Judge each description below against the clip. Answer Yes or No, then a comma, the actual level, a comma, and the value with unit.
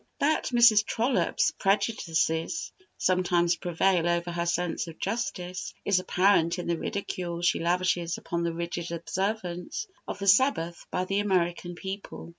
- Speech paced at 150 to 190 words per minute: No, average, 140 wpm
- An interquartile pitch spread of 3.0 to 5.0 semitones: No, narrow, 2.6 semitones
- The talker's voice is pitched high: No, medium, 180 Hz